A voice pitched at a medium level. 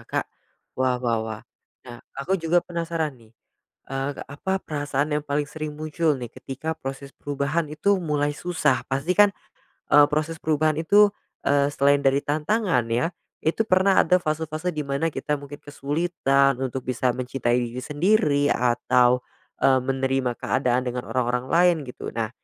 Yes: medium, 145 Hz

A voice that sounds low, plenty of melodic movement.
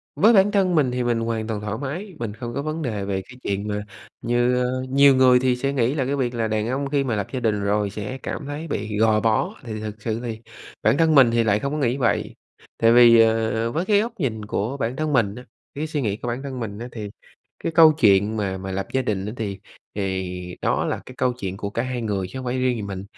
No: low, 120 Hz; average, 4.2 semitones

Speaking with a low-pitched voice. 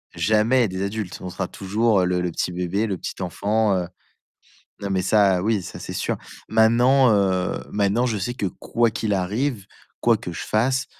Yes: low, 100 Hz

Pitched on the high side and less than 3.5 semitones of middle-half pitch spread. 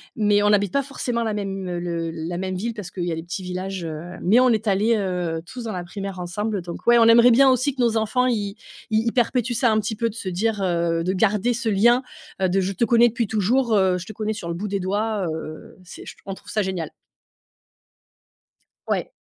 No: high, 205 Hz; average, 4.1 semitones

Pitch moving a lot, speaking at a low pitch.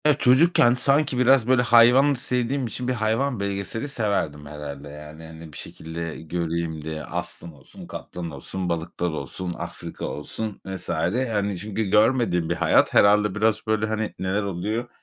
Yes: wide, 6.3 semitones; low, 100 Hz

